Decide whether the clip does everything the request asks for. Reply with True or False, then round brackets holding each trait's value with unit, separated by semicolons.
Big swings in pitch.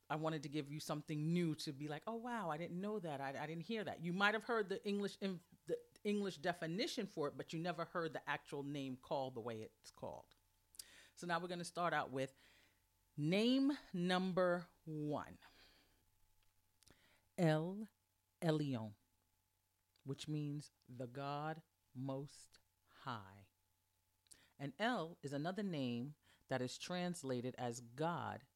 True (6.9 semitones)